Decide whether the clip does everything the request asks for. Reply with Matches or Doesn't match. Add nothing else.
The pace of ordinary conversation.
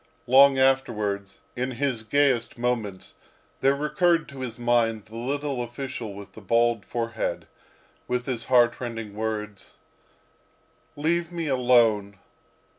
Doesn't match